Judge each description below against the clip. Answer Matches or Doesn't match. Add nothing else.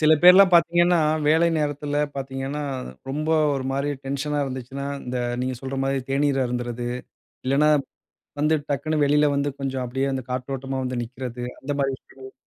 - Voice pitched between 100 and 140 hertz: Matches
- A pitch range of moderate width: Doesn't match